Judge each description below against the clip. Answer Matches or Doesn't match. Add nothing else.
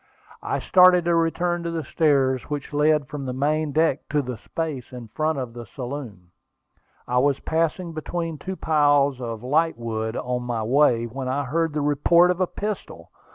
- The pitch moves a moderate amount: Matches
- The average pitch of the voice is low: Doesn't match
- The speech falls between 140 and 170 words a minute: Doesn't match